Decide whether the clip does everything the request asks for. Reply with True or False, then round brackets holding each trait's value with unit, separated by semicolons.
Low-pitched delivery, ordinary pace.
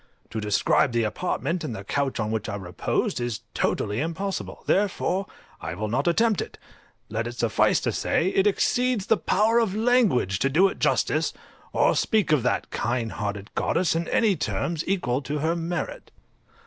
False (150 Hz; 175 wpm)